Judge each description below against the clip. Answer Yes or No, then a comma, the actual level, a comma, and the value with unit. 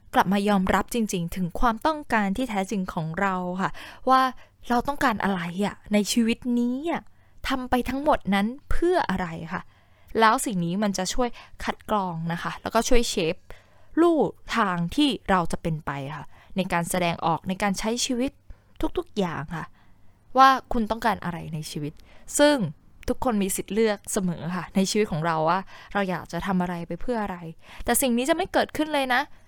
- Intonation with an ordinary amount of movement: No, wide, 5.7 semitones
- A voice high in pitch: Yes, high, 205 Hz